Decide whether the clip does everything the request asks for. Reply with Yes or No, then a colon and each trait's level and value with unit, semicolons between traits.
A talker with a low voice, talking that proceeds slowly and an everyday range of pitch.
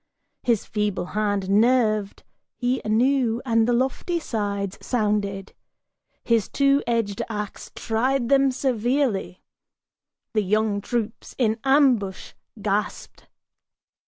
No: high, 225 Hz; slow, 100 wpm; average, 3.6 semitones